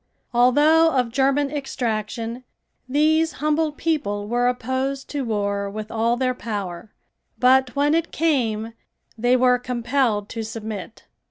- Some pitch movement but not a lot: Yes, average, 4.1 semitones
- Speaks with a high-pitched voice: Yes, very high, 250 Hz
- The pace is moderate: No, slow, 125 wpm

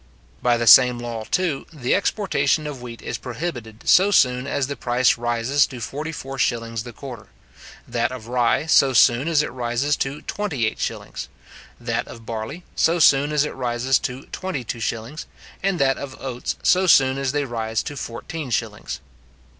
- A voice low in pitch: Yes, low, 130 Hz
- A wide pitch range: No, average, 3.5 semitones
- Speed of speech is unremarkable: Yes, average, 180 wpm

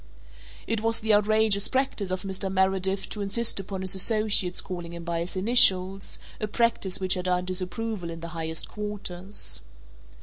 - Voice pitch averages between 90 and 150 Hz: No, high, 190 Hz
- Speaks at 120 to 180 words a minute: Yes, average, 165 wpm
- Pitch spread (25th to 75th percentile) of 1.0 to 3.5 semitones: Yes, narrow, 2.5 semitones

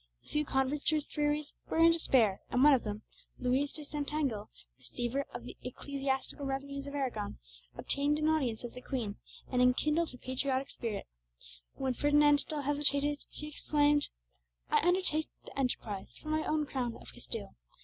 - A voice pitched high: Yes, very high, 280 Hz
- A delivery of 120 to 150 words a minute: No, average, 170 wpm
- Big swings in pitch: No, average, 2.9 semitones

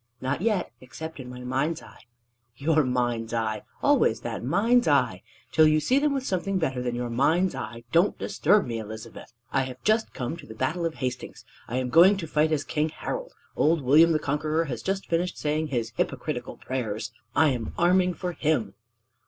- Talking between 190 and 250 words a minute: Yes, average, 195 wpm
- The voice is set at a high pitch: No, medium, 150 Hz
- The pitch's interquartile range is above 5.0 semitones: Yes, wide, 5.5 semitones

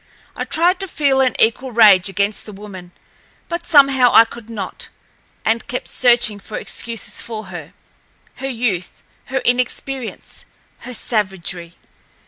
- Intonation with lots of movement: No, average, 4.5 semitones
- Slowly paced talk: Yes, slow, 130 wpm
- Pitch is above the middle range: Yes, high, 230 Hz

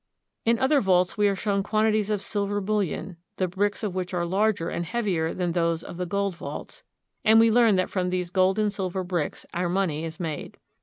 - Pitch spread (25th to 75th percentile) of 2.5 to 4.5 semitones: Yes, average, 2.9 semitones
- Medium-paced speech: No, fast, 210 wpm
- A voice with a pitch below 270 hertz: Yes, high, 190 Hz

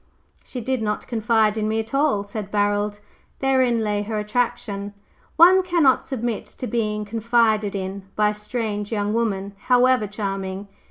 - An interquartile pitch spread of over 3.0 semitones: No, average, 2.7 semitones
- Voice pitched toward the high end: Yes, high, 215 Hz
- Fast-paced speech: No, average, 155 wpm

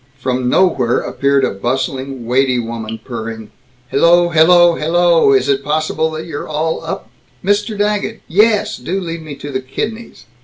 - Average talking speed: Yes, average, 155 wpm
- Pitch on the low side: No, medium, 150 Hz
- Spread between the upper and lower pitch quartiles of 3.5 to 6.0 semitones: Yes, average, 5.1 semitones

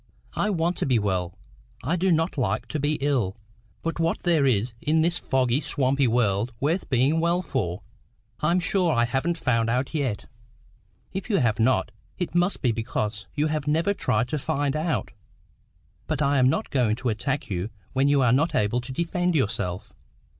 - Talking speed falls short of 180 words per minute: No, average, 185 wpm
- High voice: No, medium, 140 Hz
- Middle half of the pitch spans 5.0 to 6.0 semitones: Yes, wide, 5.6 semitones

